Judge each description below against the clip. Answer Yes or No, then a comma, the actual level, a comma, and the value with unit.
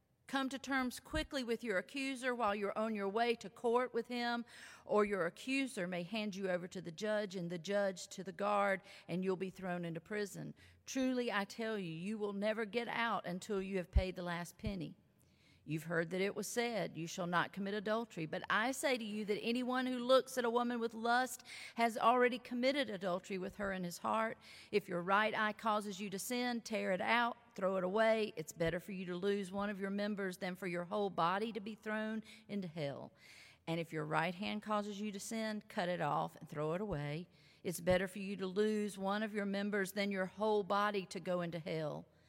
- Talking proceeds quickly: Yes, fast, 220 wpm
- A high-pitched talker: Yes, high, 205 Hz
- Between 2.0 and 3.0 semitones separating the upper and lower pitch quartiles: No, average, 3.7 semitones